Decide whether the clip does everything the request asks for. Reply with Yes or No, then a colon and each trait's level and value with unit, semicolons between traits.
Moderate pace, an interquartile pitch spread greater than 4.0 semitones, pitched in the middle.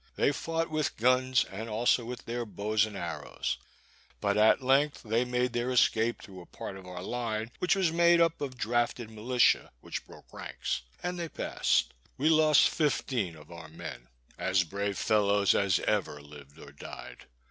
No: average, 175 wpm; average, 4.7 semitones; low, 115 Hz